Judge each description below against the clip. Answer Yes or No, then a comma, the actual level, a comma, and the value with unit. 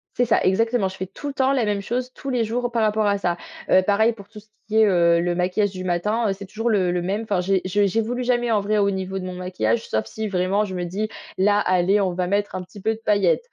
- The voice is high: Yes, high, 200 Hz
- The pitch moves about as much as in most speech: Yes, average, 3.1 semitones